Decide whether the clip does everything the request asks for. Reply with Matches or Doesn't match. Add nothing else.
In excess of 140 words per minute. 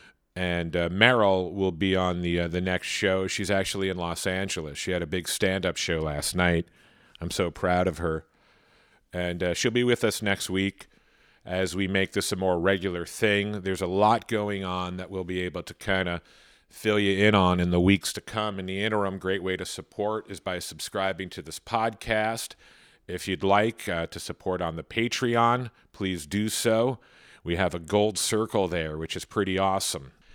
Matches